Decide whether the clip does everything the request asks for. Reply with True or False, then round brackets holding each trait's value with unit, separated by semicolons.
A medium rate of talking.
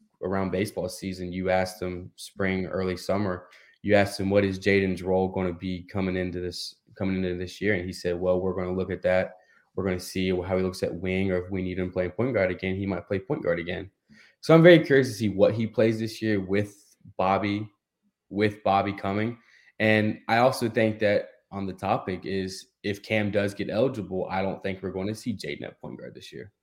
False (230 wpm)